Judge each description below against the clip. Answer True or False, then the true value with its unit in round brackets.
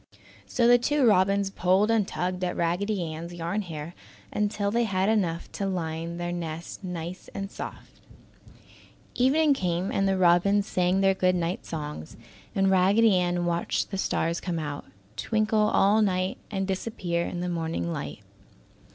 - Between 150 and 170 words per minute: True (160 wpm)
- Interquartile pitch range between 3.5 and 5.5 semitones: False (2.8 semitones)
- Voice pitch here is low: False (185 Hz)